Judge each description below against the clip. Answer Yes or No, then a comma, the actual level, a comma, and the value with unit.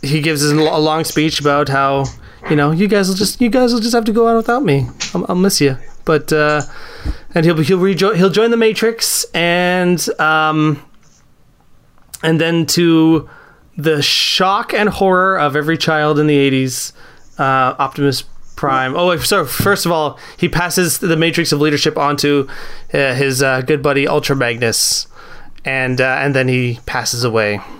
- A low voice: No, medium, 155 Hz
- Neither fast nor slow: Yes, average, 180 wpm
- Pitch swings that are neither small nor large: Yes, average, 4.2 semitones